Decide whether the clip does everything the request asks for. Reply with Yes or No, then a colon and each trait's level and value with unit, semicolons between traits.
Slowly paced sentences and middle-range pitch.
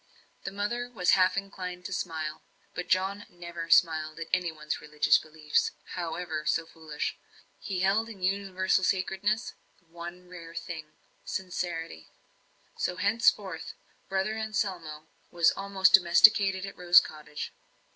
Yes: slow, 125 wpm; medium, 180 Hz